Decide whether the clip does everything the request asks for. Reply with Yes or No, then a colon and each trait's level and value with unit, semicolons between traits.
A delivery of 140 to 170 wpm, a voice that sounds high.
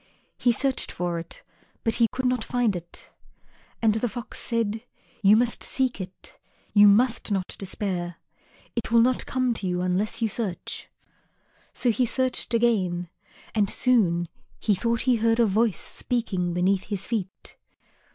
Yes: average, 150 wpm; high, 220 Hz